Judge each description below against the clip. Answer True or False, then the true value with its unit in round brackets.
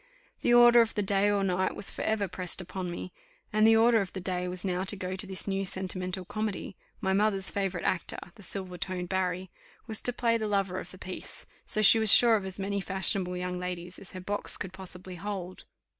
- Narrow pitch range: True (2.1 semitones)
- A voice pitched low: False (190 Hz)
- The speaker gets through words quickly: True (225 wpm)